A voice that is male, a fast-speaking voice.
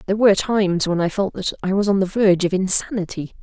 No: female; fast, 245 wpm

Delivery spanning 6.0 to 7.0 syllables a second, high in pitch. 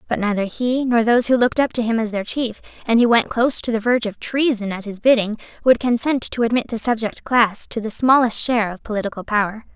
Yes: 6.1 syllables/s; high, 230 Hz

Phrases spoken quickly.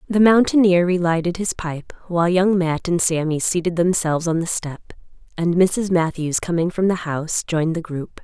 No: average, 180 wpm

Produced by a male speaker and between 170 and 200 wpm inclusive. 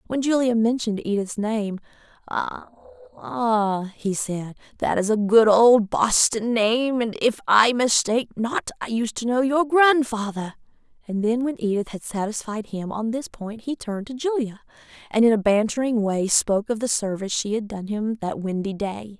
No: female; average, 175 wpm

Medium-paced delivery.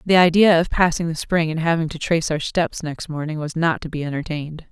No: fast, 240 wpm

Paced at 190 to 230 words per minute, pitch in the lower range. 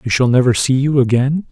No: fast, 240 wpm; low, 130 Hz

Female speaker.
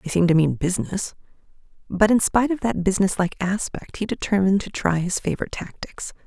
Yes: female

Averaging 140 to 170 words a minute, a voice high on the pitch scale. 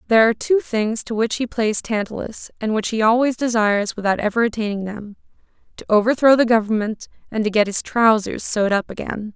No: average, 195 wpm; high, 220 Hz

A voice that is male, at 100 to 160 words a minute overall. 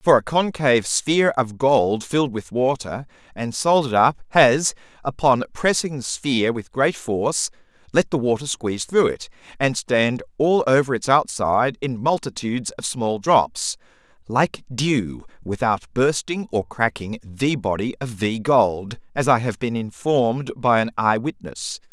Yes: male; average, 155 wpm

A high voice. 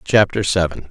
No: very low, 95 Hz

